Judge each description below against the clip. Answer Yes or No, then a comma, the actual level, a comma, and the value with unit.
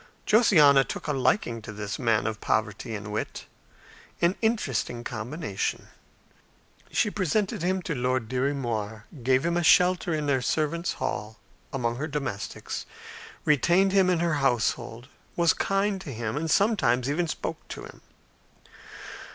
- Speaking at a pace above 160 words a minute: No, average, 145 wpm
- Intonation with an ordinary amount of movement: No, wide, 6.7 semitones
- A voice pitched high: No, medium, 140 Hz